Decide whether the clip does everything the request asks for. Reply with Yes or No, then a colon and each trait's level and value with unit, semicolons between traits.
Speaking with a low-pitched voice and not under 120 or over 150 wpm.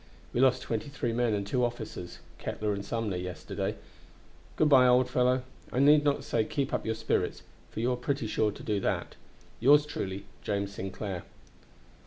No: low, 115 Hz; average, 180 wpm